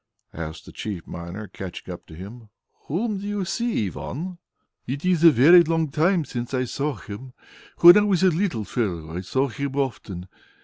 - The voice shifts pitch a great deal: Yes, wide, 9.0 semitones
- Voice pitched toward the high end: No, low, 135 Hz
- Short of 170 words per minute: No, average, 180 wpm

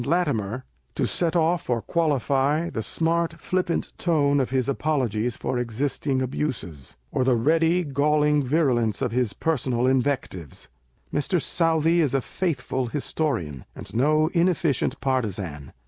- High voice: No, medium, 140 Hz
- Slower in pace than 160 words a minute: Yes, slow, 135 wpm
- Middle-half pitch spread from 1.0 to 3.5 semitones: No, average, 4.9 semitones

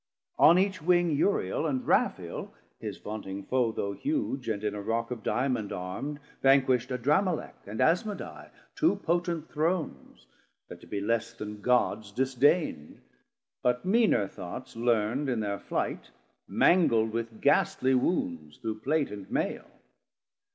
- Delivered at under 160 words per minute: Yes, slow, 135 wpm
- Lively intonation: Yes, wide, 6.5 semitones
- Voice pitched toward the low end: Yes, low, 125 Hz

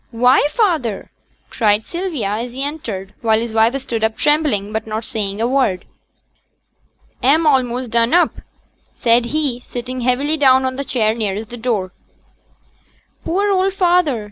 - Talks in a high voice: Yes, high, 245 Hz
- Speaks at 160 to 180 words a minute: No, average, 150 wpm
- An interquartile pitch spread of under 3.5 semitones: No, average, 4.7 semitones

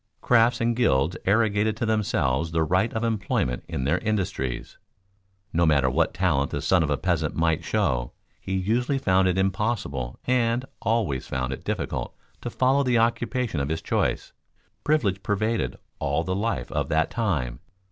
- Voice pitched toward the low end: Yes, very low, 95 Hz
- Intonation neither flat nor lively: No, wide, 7.1 semitones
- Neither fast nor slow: Yes, average, 165 wpm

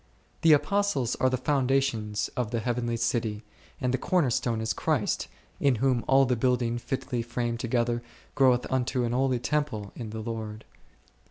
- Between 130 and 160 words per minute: No, average, 170 wpm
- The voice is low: Yes, low, 120 Hz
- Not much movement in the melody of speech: Yes, narrow, 2.3 semitones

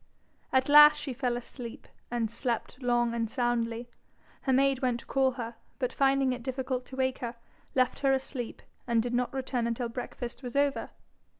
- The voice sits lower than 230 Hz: No, very high, 250 Hz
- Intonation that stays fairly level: Yes, narrow, 1.9 semitones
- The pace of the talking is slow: No, average, 180 wpm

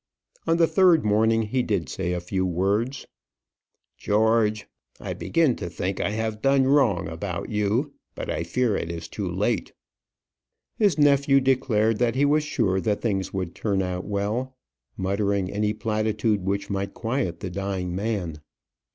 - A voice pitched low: Yes, low, 105 Hz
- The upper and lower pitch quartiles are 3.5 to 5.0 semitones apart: Yes, average, 4.4 semitones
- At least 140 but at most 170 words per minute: Yes, average, 160 wpm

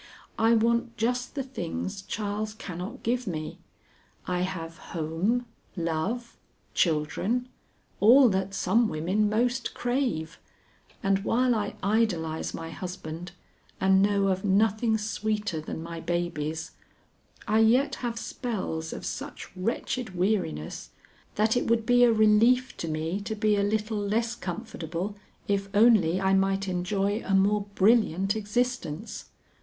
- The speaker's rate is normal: No, slow, 130 wpm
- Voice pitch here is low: No, high, 205 Hz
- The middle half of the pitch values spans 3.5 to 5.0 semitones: Yes, average, 4.2 semitones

